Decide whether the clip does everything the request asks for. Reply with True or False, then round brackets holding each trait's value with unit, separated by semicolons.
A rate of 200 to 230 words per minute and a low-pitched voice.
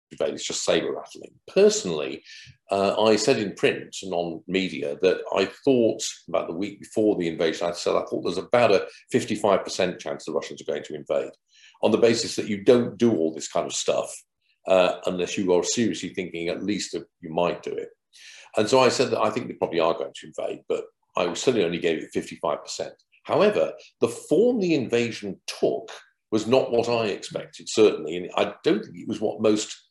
True (205 wpm; 120 Hz)